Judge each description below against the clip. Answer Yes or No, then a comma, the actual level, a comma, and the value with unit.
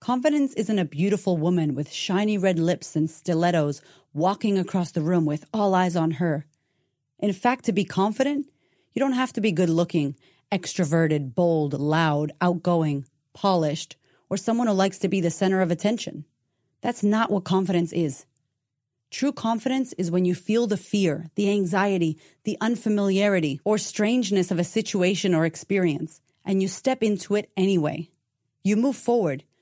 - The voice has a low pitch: No, medium, 180 Hz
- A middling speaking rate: Yes, average, 160 wpm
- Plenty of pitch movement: No, average, 4.6 semitones